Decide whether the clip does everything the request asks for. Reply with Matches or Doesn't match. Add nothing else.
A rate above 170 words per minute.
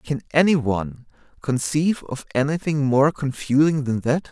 Doesn't match